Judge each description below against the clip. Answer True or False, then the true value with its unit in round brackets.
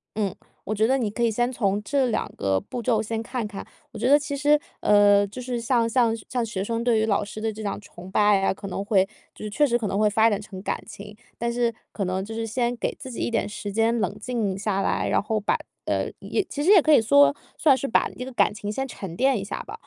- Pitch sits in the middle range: False (220 Hz)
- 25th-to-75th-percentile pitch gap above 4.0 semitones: False (3.2 semitones)